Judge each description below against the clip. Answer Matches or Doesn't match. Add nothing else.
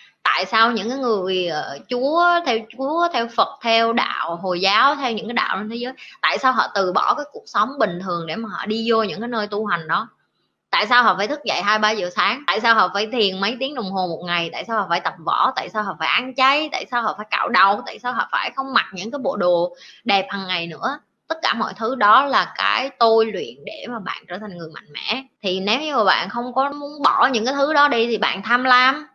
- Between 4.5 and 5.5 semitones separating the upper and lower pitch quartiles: Matches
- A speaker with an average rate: Doesn't match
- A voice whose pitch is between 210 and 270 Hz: Matches